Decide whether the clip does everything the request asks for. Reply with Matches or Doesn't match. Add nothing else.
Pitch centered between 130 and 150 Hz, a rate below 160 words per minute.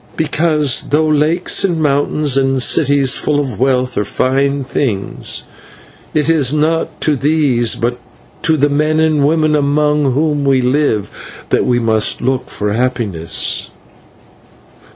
Matches